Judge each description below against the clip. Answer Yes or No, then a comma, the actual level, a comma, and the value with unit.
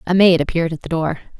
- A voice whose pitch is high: No, medium, 165 Hz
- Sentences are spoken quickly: Yes, fast, 260 wpm